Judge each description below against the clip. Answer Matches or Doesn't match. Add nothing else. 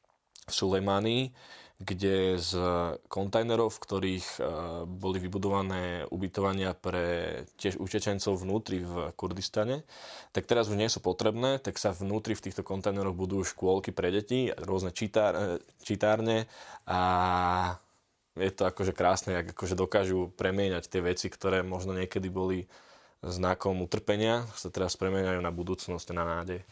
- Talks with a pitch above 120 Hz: Doesn't match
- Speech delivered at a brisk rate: Doesn't match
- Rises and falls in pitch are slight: Matches